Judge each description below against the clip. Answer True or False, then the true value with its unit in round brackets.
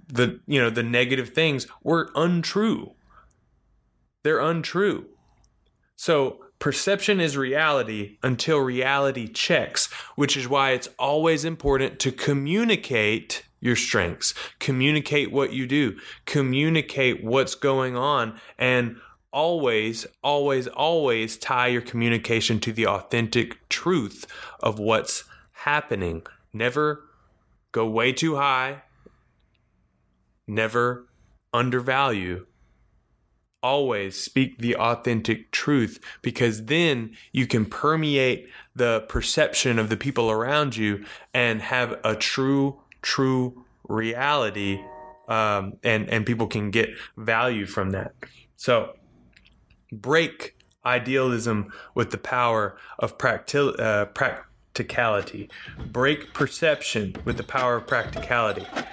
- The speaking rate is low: True (105 wpm)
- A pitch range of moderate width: True (3.9 semitones)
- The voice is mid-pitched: False (125 Hz)